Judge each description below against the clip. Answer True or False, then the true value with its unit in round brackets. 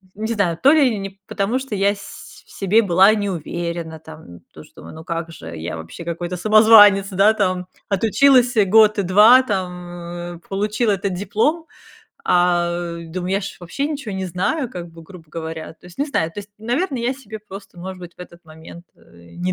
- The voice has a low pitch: False (190 Hz)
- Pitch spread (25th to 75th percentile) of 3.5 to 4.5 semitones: True (3.9 semitones)